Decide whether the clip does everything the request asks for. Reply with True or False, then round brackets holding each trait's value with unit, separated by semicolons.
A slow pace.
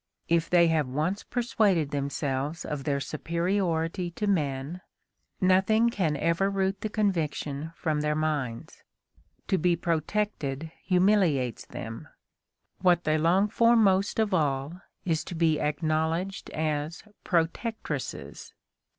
True (120 wpm)